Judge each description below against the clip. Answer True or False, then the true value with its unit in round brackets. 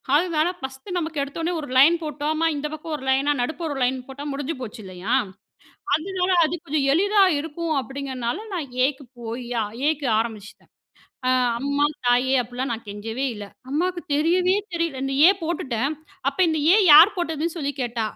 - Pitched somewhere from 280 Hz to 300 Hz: True (285 Hz)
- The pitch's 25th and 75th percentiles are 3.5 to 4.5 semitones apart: True (4.2 semitones)